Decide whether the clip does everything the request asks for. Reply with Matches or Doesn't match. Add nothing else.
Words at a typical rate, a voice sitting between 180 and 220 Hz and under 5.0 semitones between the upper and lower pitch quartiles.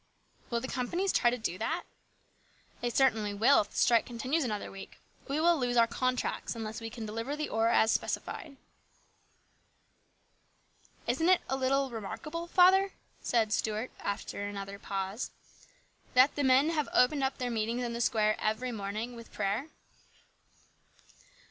Doesn't match